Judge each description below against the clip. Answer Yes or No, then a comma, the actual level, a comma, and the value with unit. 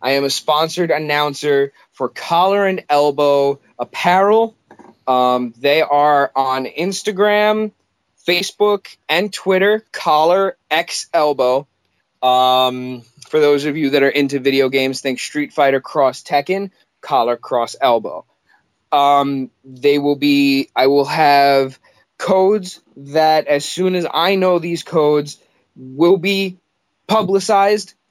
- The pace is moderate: No, slow, 125 wpm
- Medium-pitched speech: Yes, medium, 145 Hz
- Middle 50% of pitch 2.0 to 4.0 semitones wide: No, average, 5.3 semitones